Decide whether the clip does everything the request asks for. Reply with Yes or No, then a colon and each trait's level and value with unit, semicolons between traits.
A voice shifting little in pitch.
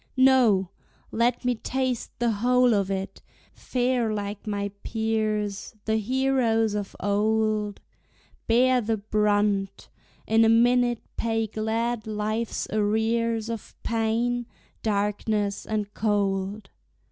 Yes: narrow, 2.2 semitones